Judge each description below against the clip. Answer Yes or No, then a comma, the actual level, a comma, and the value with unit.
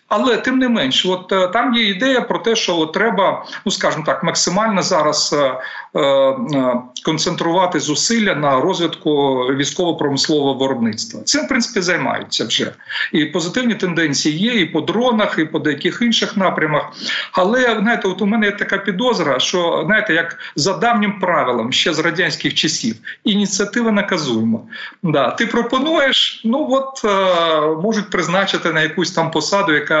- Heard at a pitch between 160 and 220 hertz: Yes, medium, 185 Hz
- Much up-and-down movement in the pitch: Yes, wide, 5.9 semitones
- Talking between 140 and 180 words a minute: Yes, average, 150 wpm